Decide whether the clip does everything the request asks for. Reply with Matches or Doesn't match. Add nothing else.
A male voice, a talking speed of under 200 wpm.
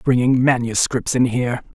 Matches